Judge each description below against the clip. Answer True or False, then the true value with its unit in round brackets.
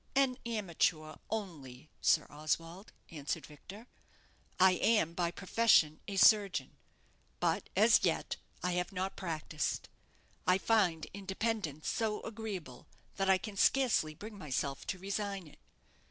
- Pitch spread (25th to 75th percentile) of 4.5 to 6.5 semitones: True (5.2 semitones)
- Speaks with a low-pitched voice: False (185 Hz)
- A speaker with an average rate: False (125 wpm)